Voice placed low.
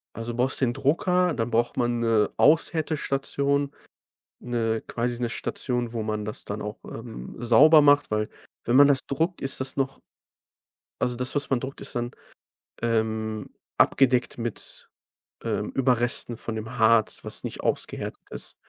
Yes: low, 120 Hz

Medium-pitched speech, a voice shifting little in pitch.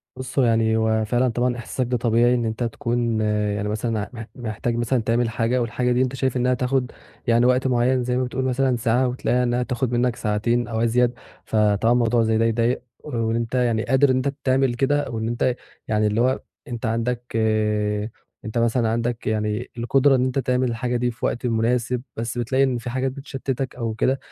No: low, 120 Hz; narrow, 1.9 semitones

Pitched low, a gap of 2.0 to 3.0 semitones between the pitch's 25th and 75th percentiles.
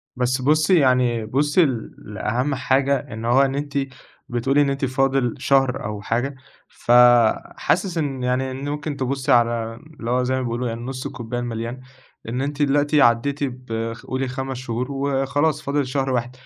Yes: low, 130 Hz; narrow, 2.5 semitones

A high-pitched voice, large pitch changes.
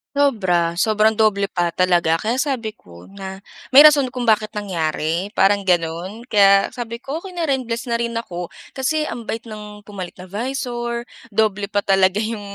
No: high, 210 Hz; average, 4.0 semitones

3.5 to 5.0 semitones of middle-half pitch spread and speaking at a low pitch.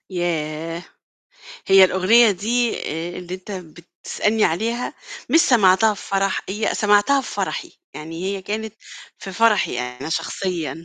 No: average, 4.1 semitones; high, 190 Hz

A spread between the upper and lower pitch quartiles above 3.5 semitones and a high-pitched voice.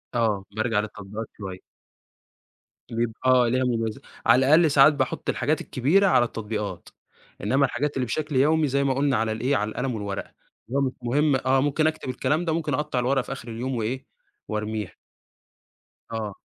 No: average, 4.0 semitones; low, 125 Hz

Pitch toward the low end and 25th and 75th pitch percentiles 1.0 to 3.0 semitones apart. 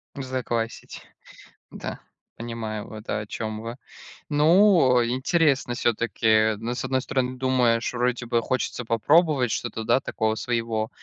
Yes: low, 120 Hz; narrow, 2.5 semitones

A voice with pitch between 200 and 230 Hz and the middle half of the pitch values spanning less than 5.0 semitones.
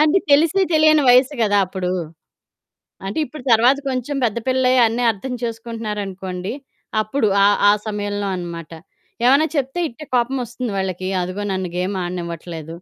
No: high, 220 Hz; wide, 5.6 semitones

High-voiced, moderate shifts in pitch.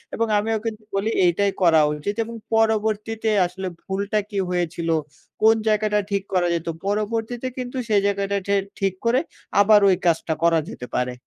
Yes: high, 205 Hz; average, 3.4 semitones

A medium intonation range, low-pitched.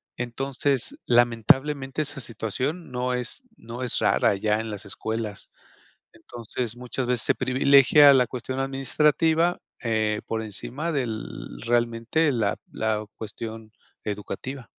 Yes: average, 3.4 semitones; low, 125 Hz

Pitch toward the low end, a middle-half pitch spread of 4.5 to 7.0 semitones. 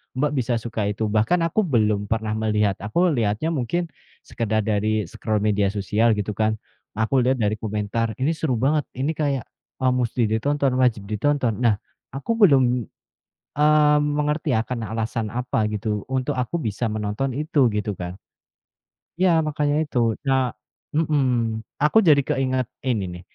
Yes: low, 120 Hz; average, 5.0 semitones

